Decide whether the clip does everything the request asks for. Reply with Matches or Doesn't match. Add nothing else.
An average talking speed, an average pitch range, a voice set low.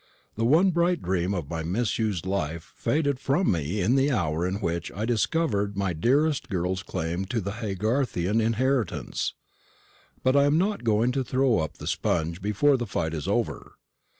Doesn't match